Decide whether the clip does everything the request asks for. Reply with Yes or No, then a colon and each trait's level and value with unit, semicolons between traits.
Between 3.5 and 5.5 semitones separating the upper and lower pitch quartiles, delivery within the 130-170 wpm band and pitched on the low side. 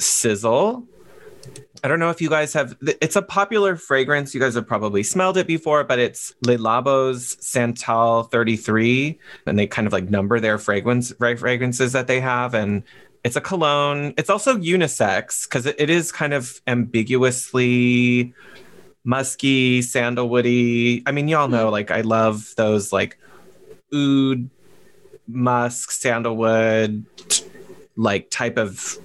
Yes: average, 3.8 semitones; average, 140 wpm; low, 125 Hz